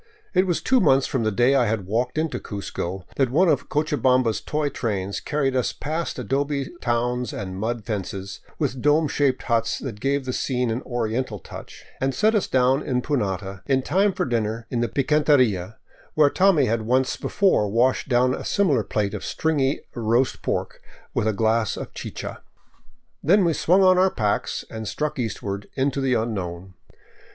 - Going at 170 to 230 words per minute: Yes, average, 180 wpm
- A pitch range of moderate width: Yes, average, 4.7 semitones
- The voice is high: No, low, 125 Hz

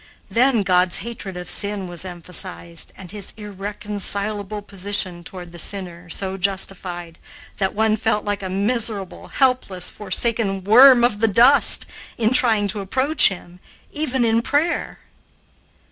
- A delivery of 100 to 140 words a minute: Yes, slow, 135 wpm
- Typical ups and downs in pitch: Yes, average, 3.4 semitones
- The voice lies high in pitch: Yes, high, 200 Hz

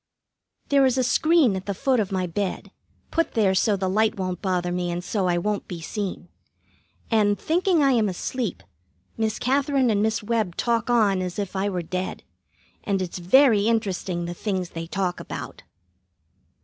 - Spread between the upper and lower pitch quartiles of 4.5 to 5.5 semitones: No, average, 4.1 semitones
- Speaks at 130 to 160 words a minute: No, average, 180 wpm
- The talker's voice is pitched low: No, high, 205 Hz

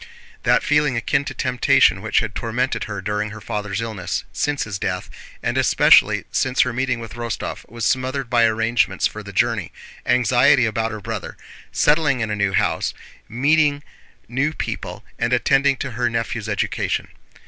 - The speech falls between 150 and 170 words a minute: Yes, average, 165 wpm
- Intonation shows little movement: No, average, 3.3 semitones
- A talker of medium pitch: No, low, 120 Hz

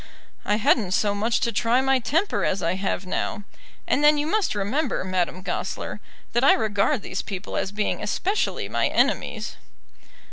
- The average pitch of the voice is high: Yes, high, 215 Hz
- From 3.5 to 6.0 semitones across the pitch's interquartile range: Yes, wide, 5.5 semitones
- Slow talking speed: No, average, 170 wpm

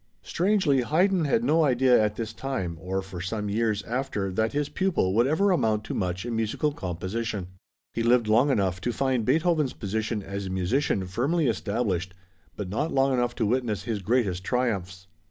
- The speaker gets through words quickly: No, average, 180 wpm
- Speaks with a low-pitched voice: Yes, low, 115 Hz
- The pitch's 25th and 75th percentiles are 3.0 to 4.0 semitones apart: No, wide, 5.5 semitones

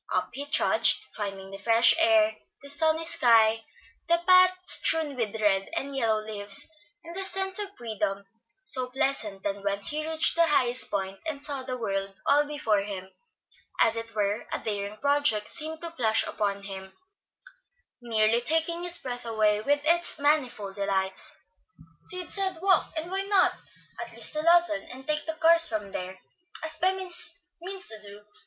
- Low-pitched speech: No, very high, 255 Hz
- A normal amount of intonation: No, wide, 7.8 semitones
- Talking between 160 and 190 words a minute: Yes, average, 170 wpm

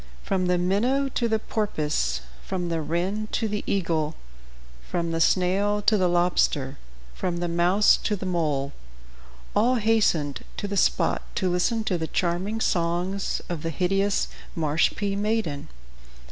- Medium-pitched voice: Yes, medium, 180 Hz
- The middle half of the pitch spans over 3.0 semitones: Yes, average, 3.6 semitones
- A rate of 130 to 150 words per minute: Yes, average, 145 wpm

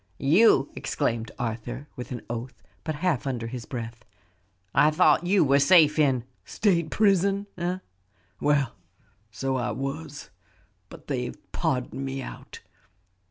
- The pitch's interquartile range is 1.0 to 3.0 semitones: No, average, 4.7 semitones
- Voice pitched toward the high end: No, medium, 140 Hz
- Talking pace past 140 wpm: No, slow, 135 wpm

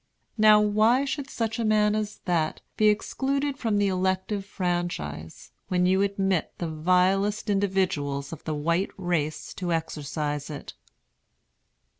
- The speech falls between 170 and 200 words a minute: No, slow, 135 wpm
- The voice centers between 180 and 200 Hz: Yes, high, 190 Hz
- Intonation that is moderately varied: Yes, average, 4.4 semitones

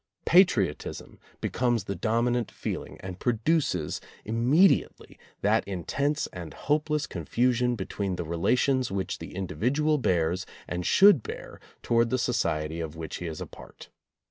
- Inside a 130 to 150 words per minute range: Yes, average, 145 wpm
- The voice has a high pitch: No, low, 115 Hz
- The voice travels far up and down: Yes, wide, 6.4 semitones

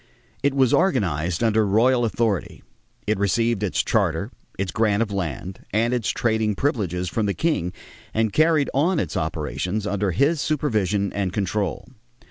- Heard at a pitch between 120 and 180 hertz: No, low, 105 Hz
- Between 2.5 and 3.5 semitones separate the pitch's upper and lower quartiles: No, average, 4.1 semitones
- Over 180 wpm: No, average, 150 wpm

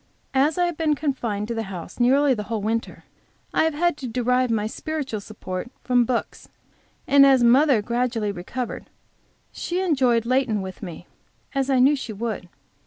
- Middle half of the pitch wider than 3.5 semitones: Yes, average, 4.0 semitones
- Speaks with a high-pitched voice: Yes, high, 245 Hz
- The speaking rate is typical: Yes, average, 175 wpm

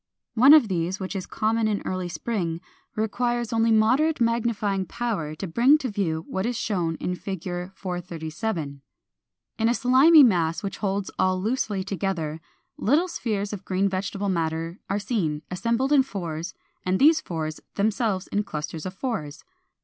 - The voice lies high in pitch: Yes, high, 195 Hz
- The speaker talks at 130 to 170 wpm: Yes, average, 155 wpm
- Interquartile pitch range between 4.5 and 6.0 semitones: Yes, average, 4.8 semitones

